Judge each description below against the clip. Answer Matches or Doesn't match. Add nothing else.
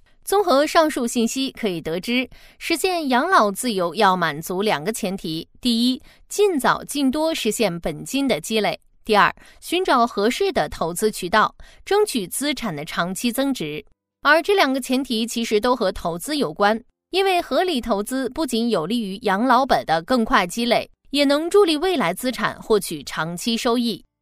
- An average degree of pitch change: Doesn't match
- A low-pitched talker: Doesn't match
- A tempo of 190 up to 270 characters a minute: Matches